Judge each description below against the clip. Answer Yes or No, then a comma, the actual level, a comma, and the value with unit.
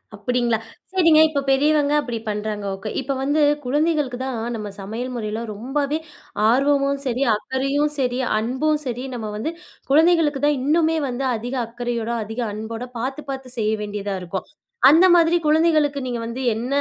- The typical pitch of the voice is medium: No, very high, 260 Hz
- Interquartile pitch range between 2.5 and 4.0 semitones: No, average, 4.4 semitones